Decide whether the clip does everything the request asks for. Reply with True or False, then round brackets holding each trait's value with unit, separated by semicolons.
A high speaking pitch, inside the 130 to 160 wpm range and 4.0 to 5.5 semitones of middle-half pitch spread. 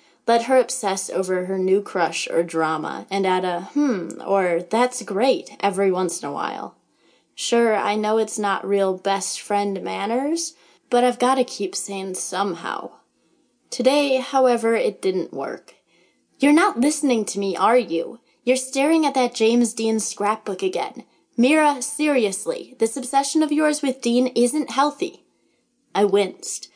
True (230 Hz; 155 wpm; 5.2 semitones)